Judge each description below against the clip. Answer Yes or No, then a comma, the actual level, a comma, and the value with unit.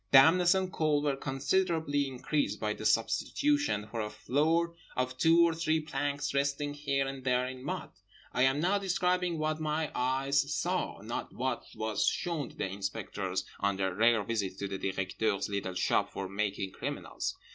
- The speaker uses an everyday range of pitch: No, wide, 6.7 semitones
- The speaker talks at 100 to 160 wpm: No, average, 170 wpm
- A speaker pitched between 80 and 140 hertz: Yes, low, 135 Hz